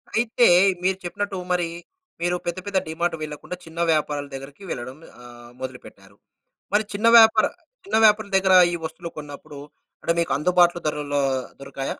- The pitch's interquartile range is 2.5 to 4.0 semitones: No, average, 4.9 semitones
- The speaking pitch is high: No, medium, 170 Hz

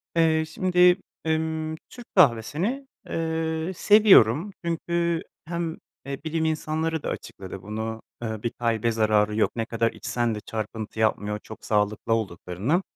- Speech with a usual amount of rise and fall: No, wide, 6.9 semitones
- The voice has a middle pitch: Yes, medium, 145 Hz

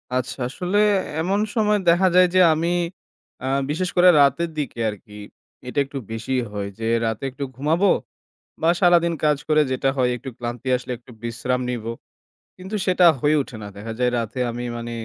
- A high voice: No, medium, 140 Hz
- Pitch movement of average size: No, wide, 6.4 semitones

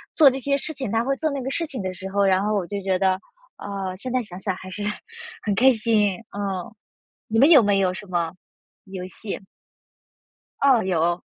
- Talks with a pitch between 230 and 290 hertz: No, high, 205 Hz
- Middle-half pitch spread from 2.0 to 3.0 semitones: No, average, 5.1 semitones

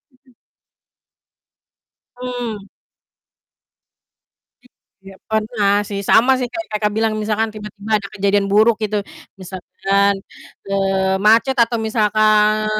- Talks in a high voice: Yes, high, 215 Hz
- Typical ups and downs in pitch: No, narrow, 1.8 semitones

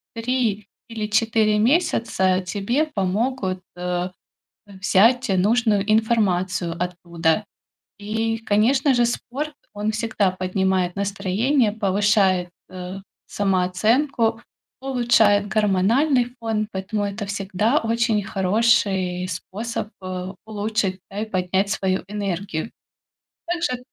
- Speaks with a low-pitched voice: No, high, 205 Hz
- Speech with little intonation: No, average, 3.5 semitones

